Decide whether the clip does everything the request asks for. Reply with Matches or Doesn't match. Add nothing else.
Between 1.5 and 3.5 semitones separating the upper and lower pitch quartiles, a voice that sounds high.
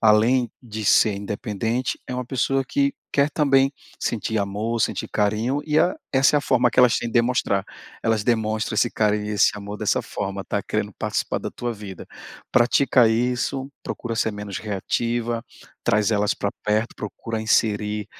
Doesn't match